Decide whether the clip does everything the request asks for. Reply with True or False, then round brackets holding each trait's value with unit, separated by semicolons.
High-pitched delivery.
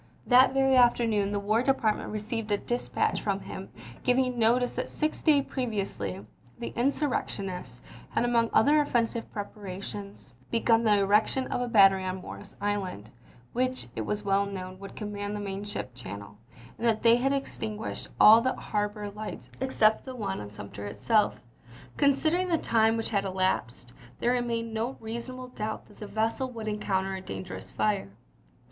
True (215 Hz)